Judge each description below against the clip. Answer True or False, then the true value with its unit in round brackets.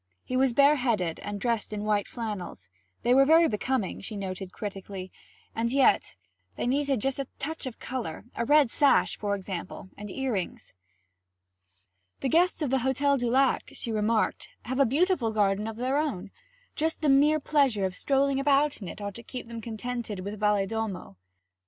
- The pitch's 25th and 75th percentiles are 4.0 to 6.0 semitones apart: True (5.0 semitones)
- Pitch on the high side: True (235 Hz)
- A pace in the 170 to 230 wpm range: True (175 wpm)